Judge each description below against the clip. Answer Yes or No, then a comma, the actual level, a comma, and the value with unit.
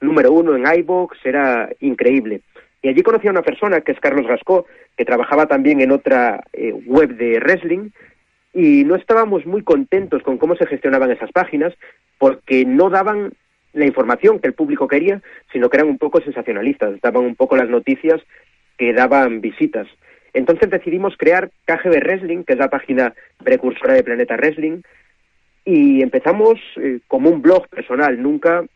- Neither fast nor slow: Yes, average, 165 wpm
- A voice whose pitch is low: No, medium, 175 Hz